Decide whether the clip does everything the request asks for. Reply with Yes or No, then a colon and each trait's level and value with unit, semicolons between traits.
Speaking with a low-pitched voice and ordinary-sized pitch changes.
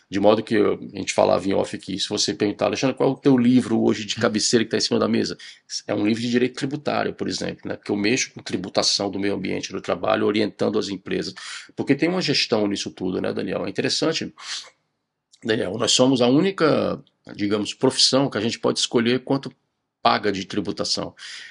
Yes: low, 115 Hz; average, 4.2 semitones